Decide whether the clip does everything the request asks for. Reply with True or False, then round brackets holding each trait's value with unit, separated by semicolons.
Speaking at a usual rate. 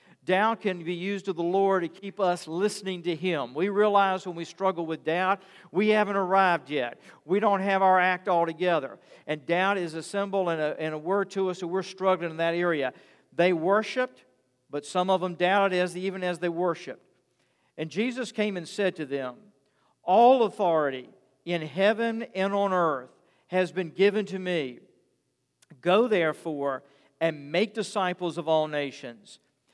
True (180 wpm)